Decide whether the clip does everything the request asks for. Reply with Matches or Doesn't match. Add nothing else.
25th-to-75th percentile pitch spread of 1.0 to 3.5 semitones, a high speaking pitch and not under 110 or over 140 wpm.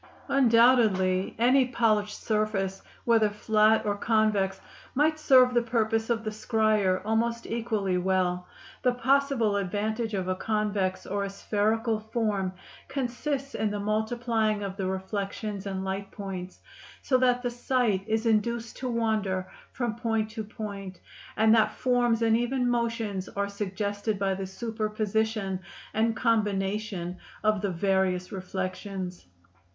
Matches